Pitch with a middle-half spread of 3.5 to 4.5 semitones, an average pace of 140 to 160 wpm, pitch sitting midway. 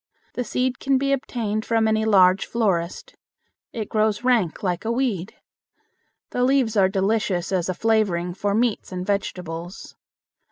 No: average, 3.9 semitones; average, 150 wpm; high, 215 Hz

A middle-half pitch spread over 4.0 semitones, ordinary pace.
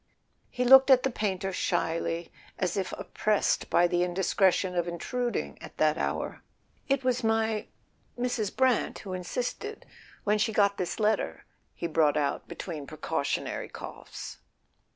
No: average, 5.3 semitones; slow, 130 wpm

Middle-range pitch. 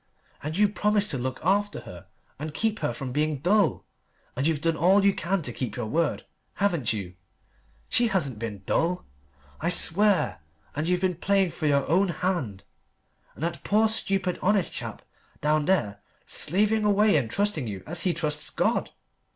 Yes: medium, 170 Hz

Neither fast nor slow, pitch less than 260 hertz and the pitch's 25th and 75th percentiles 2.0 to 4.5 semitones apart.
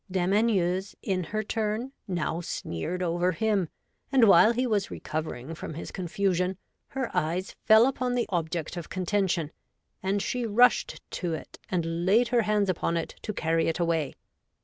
Yes: average, 165 wpm; medium, 185 Hz; average, 4.2 semitones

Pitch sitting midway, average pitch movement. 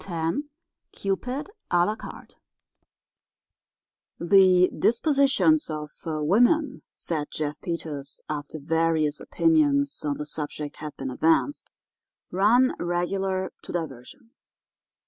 No: medium, 175 Hz; wide, 7.6 semitones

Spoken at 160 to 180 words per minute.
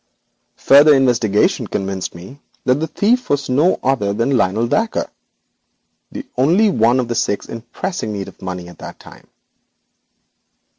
No: average, 150 wpm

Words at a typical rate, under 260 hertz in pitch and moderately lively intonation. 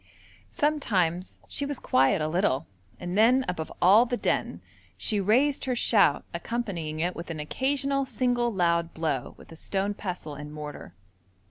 No: average, 155 wpm; high, 190 Hz; wide, 7.1 semitones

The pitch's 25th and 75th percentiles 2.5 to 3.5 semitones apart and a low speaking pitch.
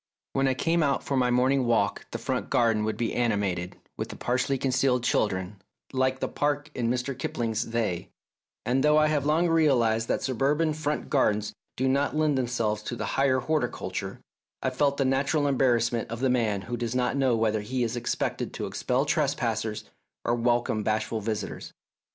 Yes: average, 3.2 semitones; low, 125 Hz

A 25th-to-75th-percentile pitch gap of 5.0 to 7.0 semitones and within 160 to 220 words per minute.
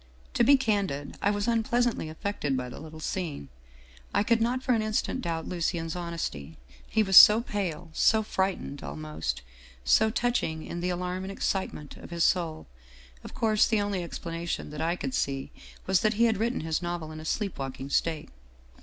Yes: wide, 5.4 semitones; average, 190 wpm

